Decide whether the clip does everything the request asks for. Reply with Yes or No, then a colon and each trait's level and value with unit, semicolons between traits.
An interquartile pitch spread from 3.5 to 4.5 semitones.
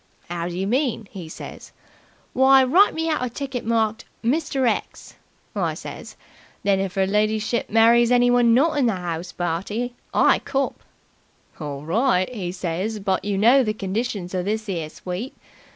No: average, 4.9 semitones